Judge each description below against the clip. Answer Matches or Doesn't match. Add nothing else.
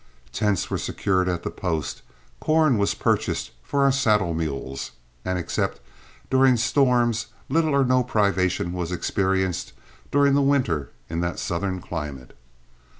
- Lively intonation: Matches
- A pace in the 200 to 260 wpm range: Doesn't match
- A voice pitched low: Matches